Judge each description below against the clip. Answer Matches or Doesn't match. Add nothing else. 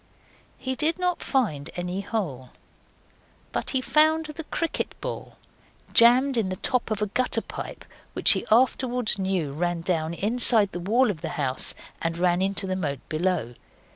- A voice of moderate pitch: Doesn't match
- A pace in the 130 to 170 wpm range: Matches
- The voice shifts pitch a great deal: Matches